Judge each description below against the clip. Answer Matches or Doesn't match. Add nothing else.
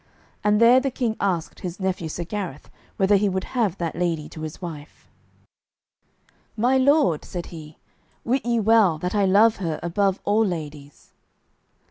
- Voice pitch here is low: Doesn't match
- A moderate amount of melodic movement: Matches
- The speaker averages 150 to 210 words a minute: Matches